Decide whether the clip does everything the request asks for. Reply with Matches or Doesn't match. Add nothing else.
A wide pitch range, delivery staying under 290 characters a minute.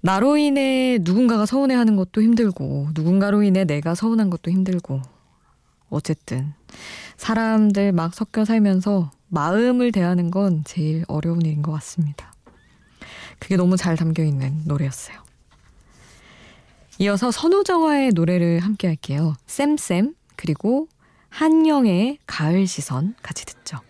Matches